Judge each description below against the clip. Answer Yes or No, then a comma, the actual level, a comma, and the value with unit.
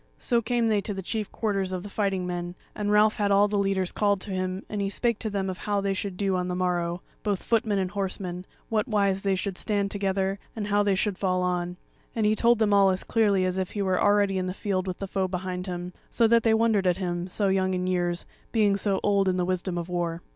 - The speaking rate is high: Yes, fast, 255 wpm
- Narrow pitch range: Yes, narrow, 2.1 semitones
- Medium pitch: No, high, 195 Hz